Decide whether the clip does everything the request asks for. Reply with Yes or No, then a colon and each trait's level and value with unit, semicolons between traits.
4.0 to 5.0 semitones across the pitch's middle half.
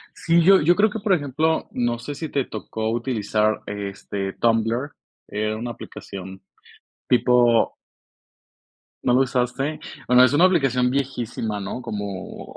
Yes: average, 4.7 semitones